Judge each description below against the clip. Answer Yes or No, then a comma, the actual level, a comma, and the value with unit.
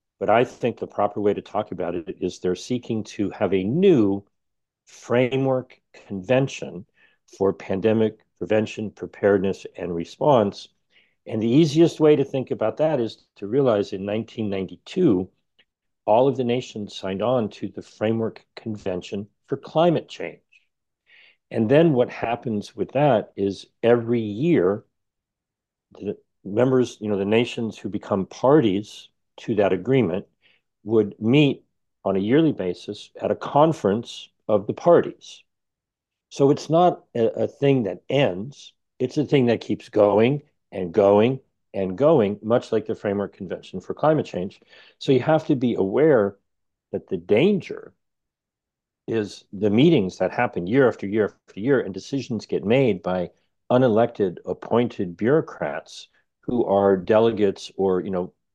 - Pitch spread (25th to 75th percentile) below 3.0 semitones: No, average, 4.2 semitones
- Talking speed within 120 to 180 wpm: Yes, slow, 145 wpm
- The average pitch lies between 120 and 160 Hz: No, low, 110 Hz